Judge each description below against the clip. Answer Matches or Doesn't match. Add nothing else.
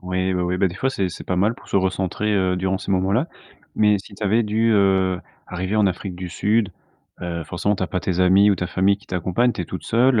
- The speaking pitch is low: Matches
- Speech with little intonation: Matches